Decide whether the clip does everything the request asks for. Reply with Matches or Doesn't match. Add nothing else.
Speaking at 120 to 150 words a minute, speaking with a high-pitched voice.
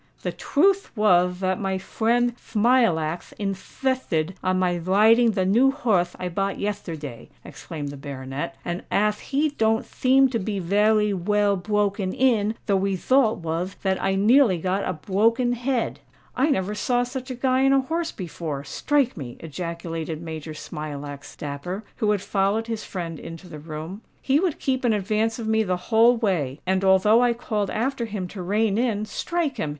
Doesn't match